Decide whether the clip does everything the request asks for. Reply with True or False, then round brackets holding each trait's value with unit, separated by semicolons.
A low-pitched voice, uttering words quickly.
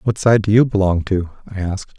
True (100 Hz; 240 wpm)